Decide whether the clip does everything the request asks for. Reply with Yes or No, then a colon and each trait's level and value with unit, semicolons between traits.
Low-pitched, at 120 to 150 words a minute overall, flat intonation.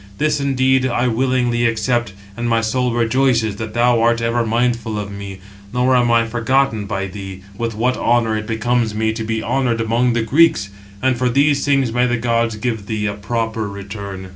No: low, 115 Hz; average, 190 wpm; narrow, 2.2 semitones